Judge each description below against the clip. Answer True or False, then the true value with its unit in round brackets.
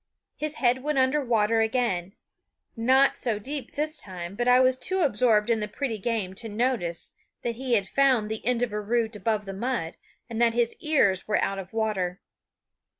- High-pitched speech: True (230 Hz)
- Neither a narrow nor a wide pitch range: True (3.7 semitones)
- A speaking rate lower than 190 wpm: False (195 wpm)